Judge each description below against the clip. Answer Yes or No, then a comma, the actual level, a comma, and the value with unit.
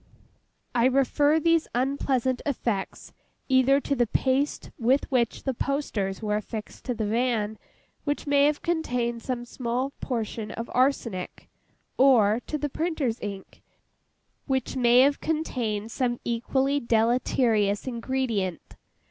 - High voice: Yes, very high, 250 Hz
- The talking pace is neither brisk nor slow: No, slow, 125 wpm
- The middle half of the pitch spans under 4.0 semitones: Yes, average, 3.3 semitones